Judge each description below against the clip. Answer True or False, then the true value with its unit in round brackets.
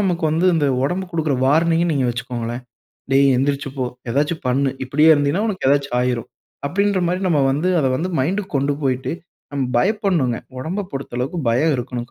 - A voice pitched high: False (145 Hz)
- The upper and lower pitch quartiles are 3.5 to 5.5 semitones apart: True (4.7 semitones)